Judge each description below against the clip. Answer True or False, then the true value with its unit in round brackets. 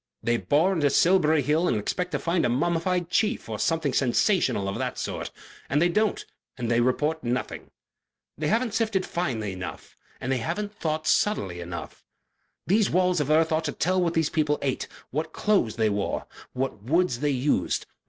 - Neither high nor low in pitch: True (155 Hz)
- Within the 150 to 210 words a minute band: True (180 wpm)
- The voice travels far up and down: True (6.3 semitones)